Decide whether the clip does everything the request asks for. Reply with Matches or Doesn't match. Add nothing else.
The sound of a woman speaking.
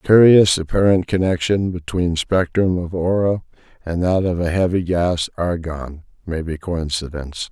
Doesn't match